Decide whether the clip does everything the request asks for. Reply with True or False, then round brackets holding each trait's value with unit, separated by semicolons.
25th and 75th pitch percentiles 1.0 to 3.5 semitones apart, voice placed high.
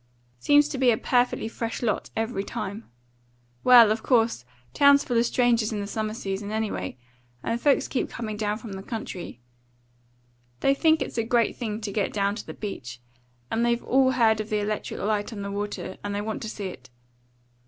True (2.6 semitones; 220 Hz)